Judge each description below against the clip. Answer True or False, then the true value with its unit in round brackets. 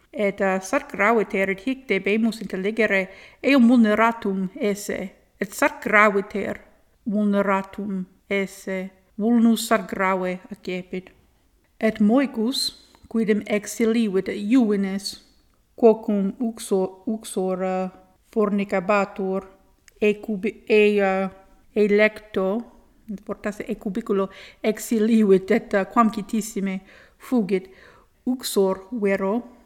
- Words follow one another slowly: True (90 wpm)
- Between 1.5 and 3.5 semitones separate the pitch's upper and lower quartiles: True (2.6 semitones)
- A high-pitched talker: True (210 Hz)